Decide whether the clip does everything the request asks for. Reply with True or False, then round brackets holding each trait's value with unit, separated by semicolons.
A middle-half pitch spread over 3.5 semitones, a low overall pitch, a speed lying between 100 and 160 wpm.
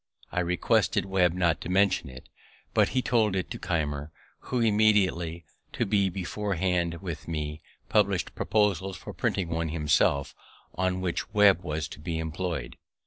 False (3.2 semitones; 90 Hz; 150 wpm)